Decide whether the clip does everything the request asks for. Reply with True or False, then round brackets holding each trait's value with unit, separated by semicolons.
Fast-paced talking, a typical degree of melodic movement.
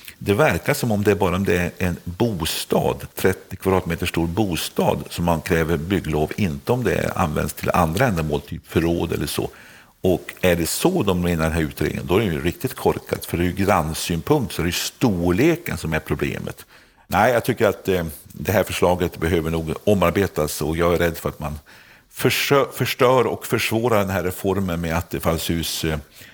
True (205 wpm; 3.0 semitones)